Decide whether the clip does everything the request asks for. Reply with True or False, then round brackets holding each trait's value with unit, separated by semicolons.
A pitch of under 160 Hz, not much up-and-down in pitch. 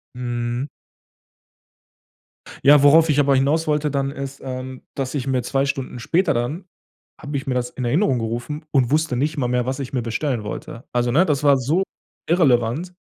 False (135 Hz; 3.2 semitones)